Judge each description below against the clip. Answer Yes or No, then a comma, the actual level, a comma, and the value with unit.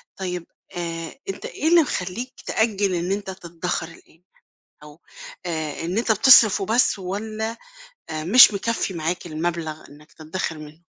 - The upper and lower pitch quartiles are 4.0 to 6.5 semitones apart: Yes, average, 4.7 semitones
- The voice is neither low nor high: Yes, medium, 180 Hz